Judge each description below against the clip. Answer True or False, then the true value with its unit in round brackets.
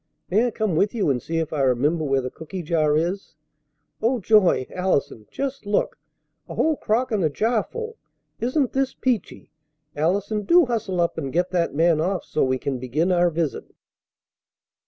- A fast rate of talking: False (180 wpm)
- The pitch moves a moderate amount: False (6.1 semitones)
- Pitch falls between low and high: True (180 Hz)